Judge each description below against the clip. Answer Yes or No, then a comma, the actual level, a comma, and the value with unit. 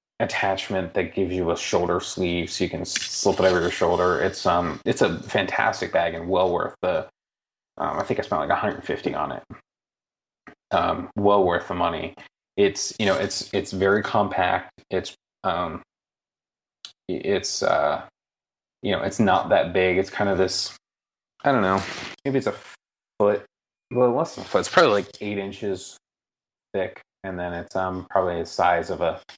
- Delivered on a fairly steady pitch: Yes, narrow, 1.6 semitones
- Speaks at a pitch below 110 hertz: Yes, very low, 95 Hz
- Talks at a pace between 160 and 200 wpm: Yes, average, 180 wpm